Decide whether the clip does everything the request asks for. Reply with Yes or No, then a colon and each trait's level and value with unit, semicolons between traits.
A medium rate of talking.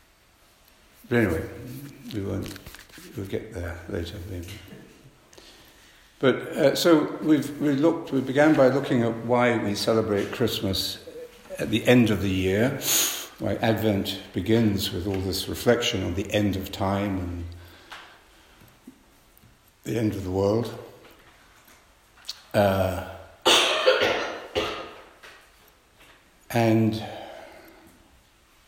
No: slow, 105 wpm